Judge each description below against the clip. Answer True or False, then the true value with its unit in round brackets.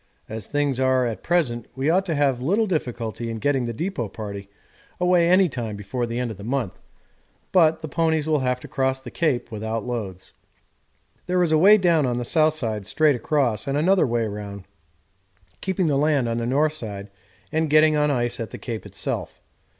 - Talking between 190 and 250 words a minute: True (200 wpm)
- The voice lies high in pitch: False (130 Hz)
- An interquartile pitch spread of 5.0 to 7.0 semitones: True (5.3 semitones)